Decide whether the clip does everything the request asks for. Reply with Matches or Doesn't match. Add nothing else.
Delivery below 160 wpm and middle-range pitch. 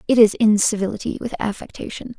Doesn't match